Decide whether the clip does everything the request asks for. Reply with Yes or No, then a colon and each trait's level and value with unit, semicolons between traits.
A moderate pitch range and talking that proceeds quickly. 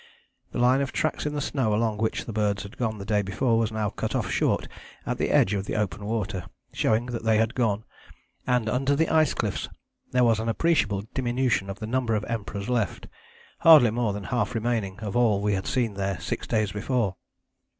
Yes: average, 3.2 semitones; fast, 215 wpm